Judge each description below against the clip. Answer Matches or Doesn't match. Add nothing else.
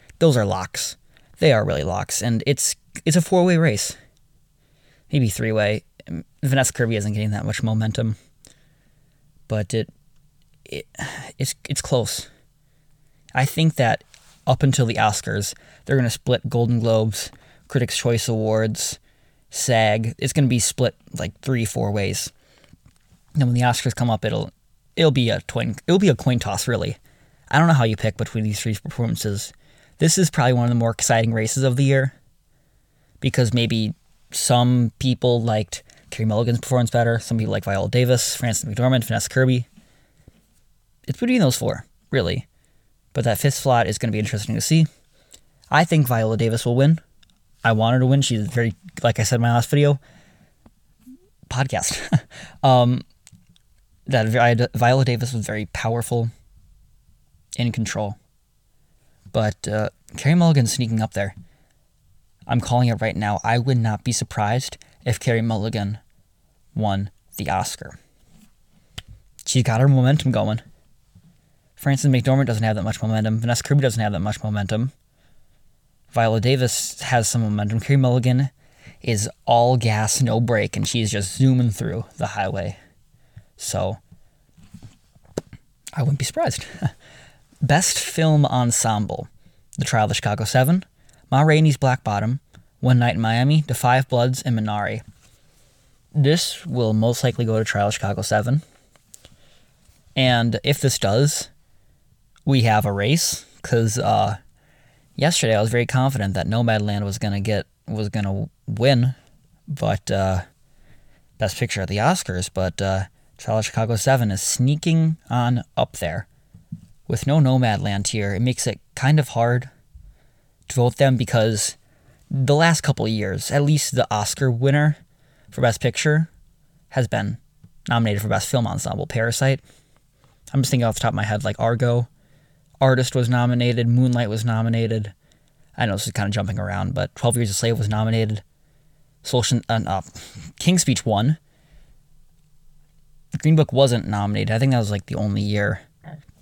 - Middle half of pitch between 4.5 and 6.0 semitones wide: Doesn't match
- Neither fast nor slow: Matches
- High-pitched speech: Doesn't match